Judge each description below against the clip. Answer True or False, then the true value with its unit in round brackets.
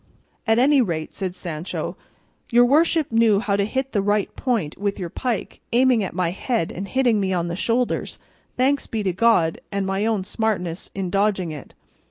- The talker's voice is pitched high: True (205 Hz)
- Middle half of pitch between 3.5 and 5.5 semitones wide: True (4.5 semitones)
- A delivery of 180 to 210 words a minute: True (190 wpm)